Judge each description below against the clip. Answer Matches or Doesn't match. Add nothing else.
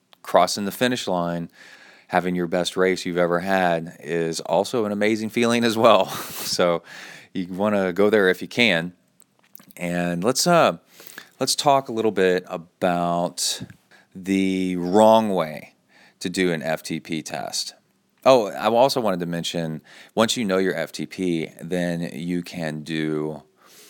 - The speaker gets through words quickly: Doesn't match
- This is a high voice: Doesn't match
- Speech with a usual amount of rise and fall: Doesn't match